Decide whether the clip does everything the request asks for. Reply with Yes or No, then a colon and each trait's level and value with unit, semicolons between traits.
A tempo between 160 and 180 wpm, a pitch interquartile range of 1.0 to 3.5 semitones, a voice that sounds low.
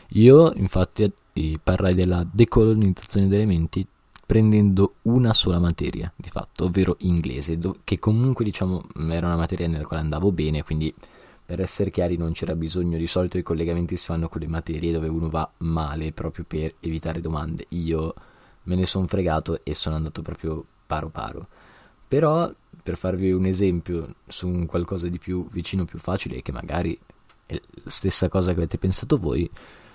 Yes: average, 165 wpm; average, 2.7 semitones; very low, 90 Hz